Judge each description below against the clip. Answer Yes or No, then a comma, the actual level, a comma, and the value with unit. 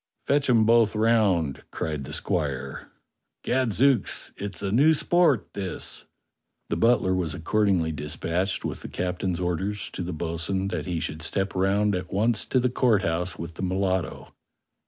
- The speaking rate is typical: Yes, average, 160 wpm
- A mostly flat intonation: No, average, 4.3 semitones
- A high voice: No, very low, 95 Hz